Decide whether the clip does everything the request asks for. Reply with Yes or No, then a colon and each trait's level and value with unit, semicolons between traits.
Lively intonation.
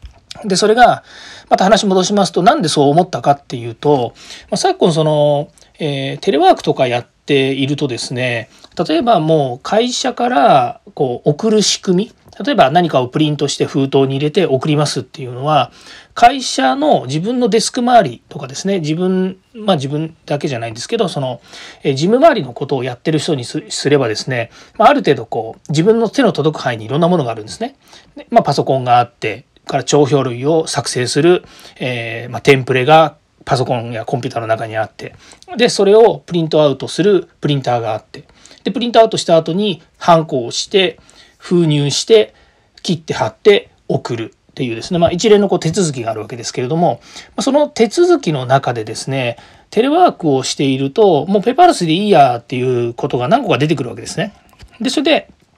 Yes: wide, 7.4 semitones